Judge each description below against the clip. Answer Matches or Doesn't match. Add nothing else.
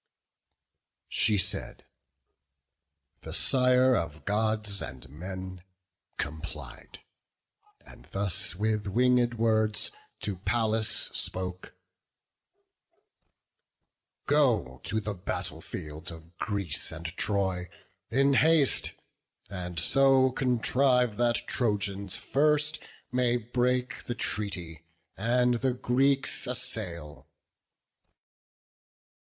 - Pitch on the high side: Doesn't match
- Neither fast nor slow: Doesn't match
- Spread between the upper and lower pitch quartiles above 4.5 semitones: Matches